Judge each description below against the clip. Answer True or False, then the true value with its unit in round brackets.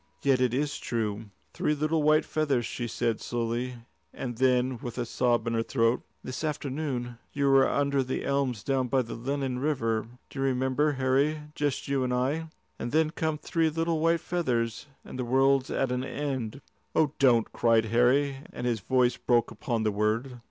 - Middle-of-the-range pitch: False (130 Hz)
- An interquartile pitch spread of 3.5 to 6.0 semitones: False (3.0 semitones)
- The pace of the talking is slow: False (185 wpm)